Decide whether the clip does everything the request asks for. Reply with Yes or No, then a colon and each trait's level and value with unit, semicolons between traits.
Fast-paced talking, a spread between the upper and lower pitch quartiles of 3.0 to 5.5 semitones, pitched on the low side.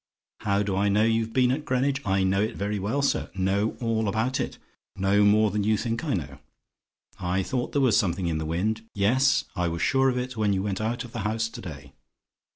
Yes: fast, 230 wpm; average, 3.7 semitones; low, 105 Hz